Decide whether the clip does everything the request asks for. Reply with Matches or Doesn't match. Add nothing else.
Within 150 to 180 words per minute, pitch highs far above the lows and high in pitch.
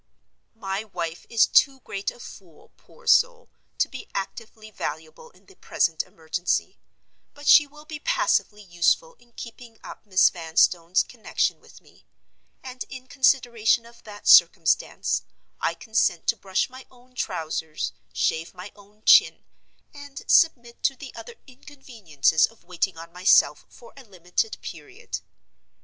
Doesn't match